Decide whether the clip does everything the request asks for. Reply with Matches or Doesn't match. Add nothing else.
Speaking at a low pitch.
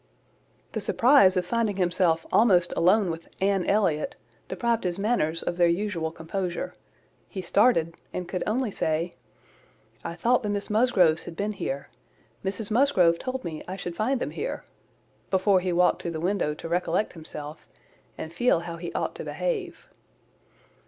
Doesn't match